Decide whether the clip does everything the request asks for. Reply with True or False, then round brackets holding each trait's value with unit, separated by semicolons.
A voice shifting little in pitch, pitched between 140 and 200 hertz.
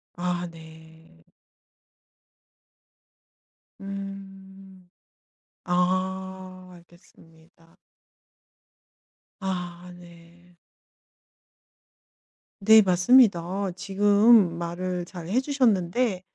True (2.2 semitones; 185 Hz)